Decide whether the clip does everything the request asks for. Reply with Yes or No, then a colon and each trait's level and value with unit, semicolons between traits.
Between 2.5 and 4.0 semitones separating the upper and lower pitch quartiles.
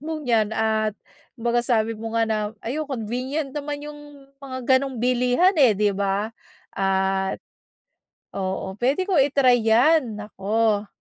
No: average, 4.4 semitones